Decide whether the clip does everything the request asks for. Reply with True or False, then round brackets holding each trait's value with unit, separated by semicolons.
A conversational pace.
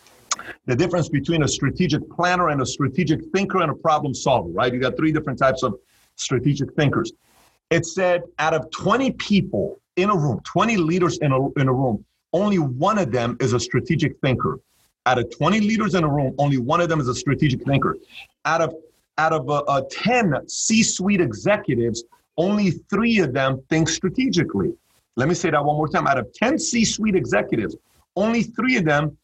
True (190 wpm)